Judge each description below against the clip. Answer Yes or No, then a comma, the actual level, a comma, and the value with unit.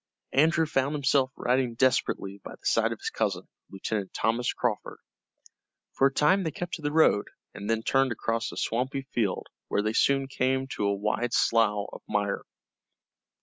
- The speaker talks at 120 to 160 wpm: No, average, 175 wpm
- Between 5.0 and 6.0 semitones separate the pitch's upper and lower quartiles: No, average, 4.1 semitones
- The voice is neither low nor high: No, low, 125 Hz